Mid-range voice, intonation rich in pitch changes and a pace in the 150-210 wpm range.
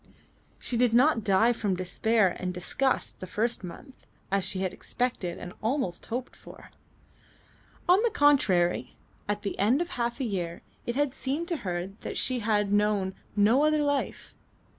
No: high, 220 Hz; wide, 5.7 semitones; average, 160 wpm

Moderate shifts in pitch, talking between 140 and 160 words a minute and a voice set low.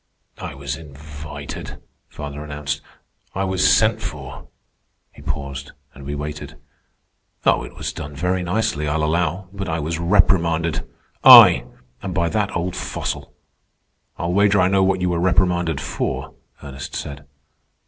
Yes: average, 4.0 semitones; average, 145 wpm; very low, 80 Hz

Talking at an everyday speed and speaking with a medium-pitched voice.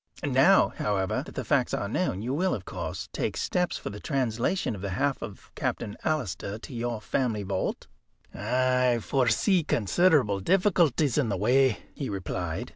No: average, 165 wpm; low, 120 Hz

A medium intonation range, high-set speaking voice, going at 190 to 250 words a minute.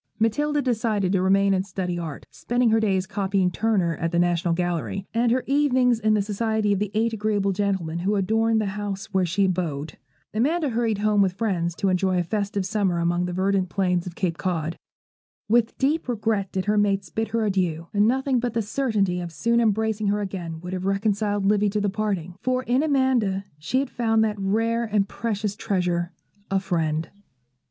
Yes: average, 3.4 semitones; high, 200 Hz; average, 195 wpm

